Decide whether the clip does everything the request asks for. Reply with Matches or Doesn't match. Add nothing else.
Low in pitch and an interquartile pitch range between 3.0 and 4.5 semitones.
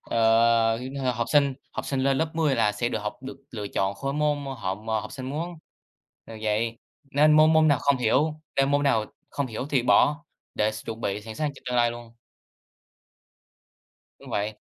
Matches